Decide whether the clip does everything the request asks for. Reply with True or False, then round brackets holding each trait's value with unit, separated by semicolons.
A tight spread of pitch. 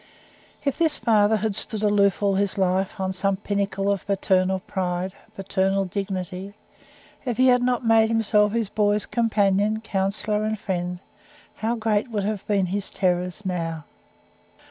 True (2.3 semitones)